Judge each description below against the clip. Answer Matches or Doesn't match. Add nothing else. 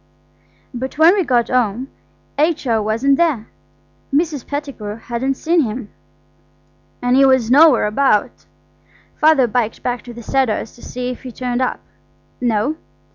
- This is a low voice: Doesn't match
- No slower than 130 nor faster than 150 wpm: Matches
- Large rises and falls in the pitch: Doesn't match